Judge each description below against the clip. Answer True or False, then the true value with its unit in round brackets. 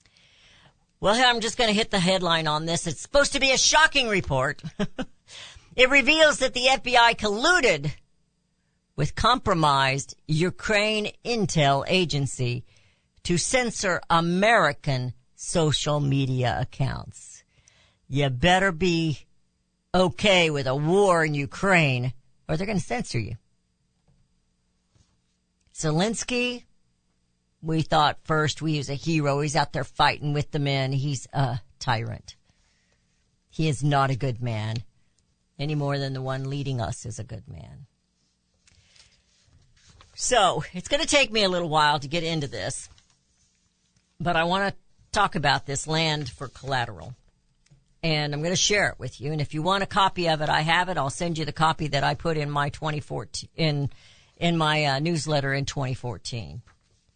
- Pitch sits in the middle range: True (150 Hz)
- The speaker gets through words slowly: False (150 wpm)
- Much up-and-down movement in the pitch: True (5.7 semitones)